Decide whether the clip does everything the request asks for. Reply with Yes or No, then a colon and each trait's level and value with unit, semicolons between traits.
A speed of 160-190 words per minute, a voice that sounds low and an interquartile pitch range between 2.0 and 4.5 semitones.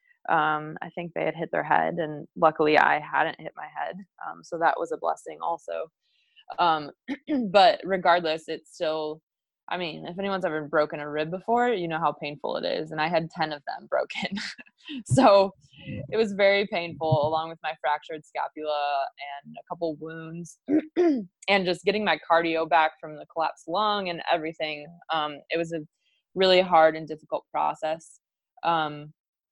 No: average, 175 wpm; medium, 165 Hz; average, 3.9 semitones